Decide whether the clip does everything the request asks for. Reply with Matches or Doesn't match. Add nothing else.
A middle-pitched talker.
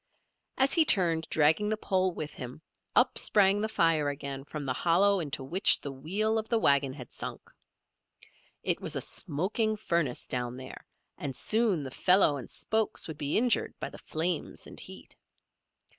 Matches